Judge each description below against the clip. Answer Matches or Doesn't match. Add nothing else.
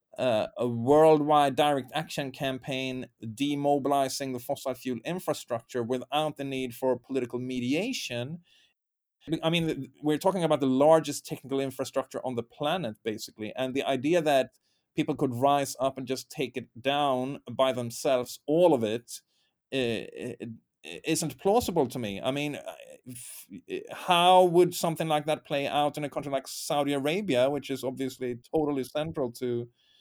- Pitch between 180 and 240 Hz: Doesn't match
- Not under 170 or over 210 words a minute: Doesn't match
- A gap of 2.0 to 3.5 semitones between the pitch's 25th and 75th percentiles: Matches